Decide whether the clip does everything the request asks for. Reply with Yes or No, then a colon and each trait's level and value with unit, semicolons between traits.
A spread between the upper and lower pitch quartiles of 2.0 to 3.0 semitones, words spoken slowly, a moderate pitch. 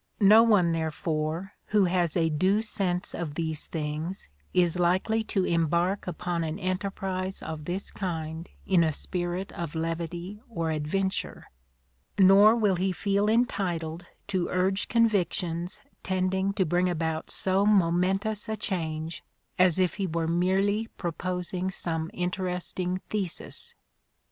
Yes: narrow, 2.6 semitones; slow, 130 wpm; medium, 180 Hz